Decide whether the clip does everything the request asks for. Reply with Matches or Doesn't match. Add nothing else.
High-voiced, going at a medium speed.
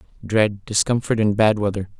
Doesn't match